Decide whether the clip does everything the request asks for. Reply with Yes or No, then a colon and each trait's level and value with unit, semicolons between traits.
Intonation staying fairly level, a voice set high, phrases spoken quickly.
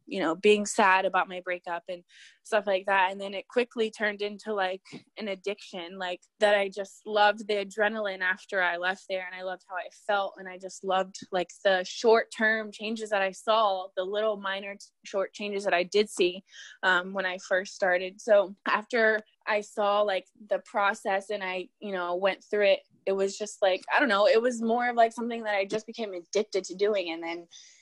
Yes: narrow, 2.3 semitones; high, 200 Hz; fast, 215 wpm